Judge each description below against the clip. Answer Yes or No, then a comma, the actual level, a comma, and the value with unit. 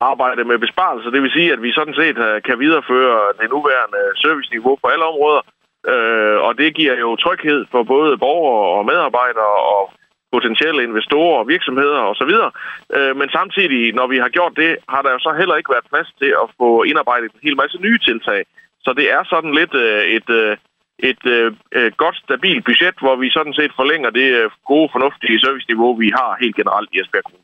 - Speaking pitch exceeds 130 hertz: Yes, medium, 140 Hz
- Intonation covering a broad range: Yes, wide, 5.7 semitones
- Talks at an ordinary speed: Yes, average, 190 wpm